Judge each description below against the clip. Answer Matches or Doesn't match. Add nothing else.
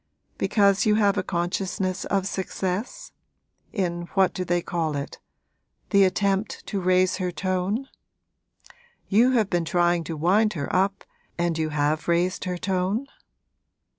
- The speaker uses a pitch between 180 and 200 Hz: Matches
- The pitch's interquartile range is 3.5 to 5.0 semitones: Doesn't match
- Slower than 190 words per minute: Matches